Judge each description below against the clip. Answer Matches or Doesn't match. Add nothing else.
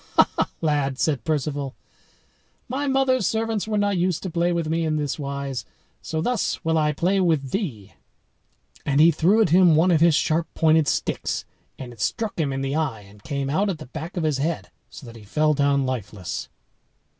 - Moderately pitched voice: Matches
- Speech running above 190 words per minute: Matches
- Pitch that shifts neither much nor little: Matches